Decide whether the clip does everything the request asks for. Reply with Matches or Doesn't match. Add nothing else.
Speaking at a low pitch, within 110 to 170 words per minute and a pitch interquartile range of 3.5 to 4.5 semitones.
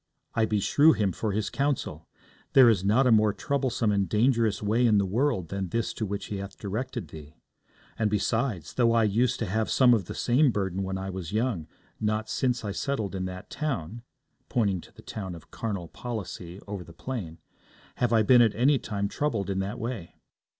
Doesn't match